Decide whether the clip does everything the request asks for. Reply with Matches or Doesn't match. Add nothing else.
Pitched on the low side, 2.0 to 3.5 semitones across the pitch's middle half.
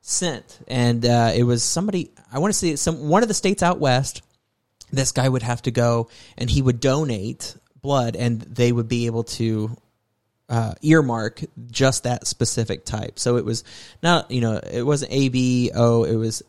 Matches